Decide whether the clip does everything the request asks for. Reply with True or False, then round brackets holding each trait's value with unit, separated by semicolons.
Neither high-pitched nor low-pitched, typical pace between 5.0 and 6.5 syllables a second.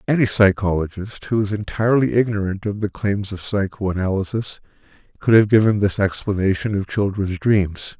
False (100 Hz; 5.1 syllables/s)